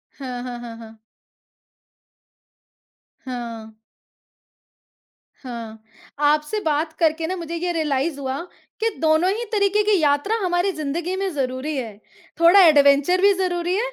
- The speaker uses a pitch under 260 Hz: No, very high, 310 Hz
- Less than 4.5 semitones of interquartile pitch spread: No, wide, 5.5 semitones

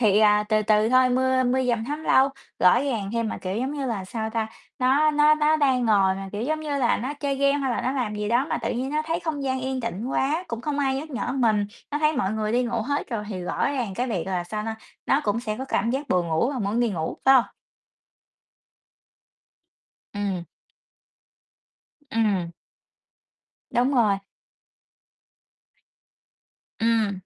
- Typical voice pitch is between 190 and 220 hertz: No, high, 240 Hz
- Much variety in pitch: No, average, 4.3 semitones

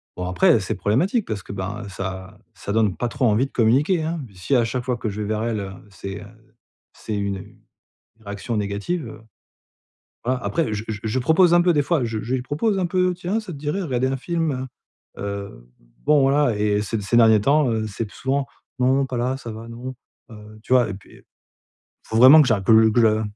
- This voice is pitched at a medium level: No, low, 115 Hz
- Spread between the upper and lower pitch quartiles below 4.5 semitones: No, average, 4.8 semitones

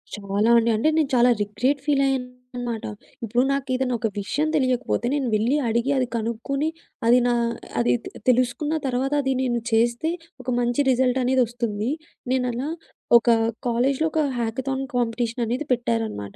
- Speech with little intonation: Yes, narrow, 2.2 semitones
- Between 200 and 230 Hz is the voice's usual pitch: No, high, 245 Hz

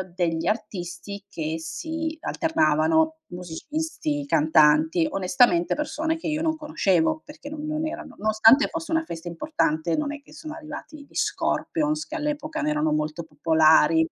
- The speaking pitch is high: Yes, very high, 280 Hz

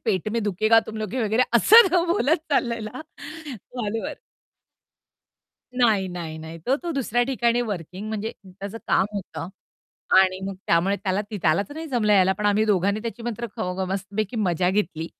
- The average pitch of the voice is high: Yes, high, 215 Hz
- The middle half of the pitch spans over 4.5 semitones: No, average, 3.8 semitones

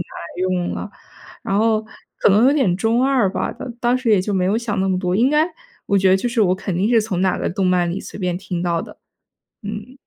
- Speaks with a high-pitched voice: Yes, high, 200 Hz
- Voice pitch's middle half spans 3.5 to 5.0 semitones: Yes, average, 4.0 semitones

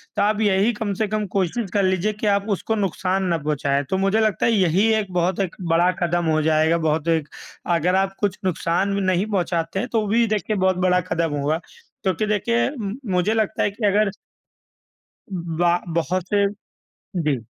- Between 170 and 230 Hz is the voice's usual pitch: Yes, high, 190 Hz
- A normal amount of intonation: Yes, average, 3.6 semitones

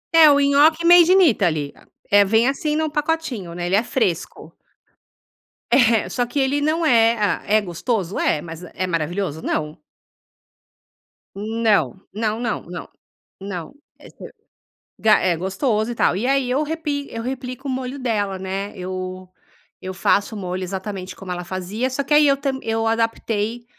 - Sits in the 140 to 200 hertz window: No, high, 220 Hz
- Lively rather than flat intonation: Yes, wide, 6.3 semitones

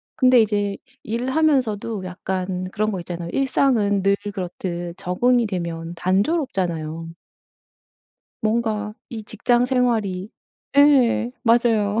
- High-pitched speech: Yes, high, 210 Hz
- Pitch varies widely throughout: No, average, 4.6 semitones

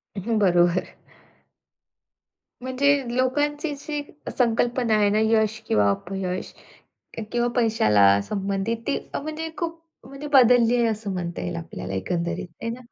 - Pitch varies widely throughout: Yes, wide, 5.8 semitones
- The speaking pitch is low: No, high, 225 Hz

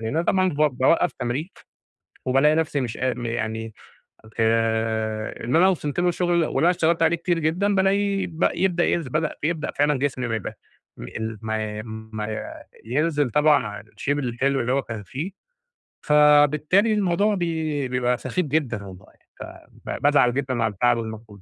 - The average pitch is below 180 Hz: Yes, medium, 140 Hz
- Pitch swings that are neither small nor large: No, wide, 6.5 semitones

